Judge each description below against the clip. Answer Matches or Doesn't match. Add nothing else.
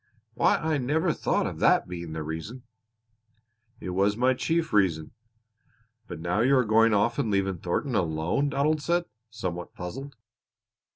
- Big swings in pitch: Matches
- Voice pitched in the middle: Doesn't match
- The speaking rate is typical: Matches